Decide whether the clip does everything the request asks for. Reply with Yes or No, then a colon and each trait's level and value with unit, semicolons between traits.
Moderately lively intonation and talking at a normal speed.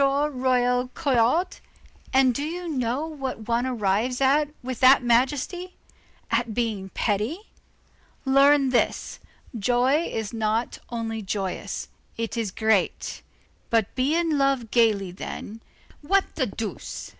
No: average, 3.8 semitones; slow, 120 wpm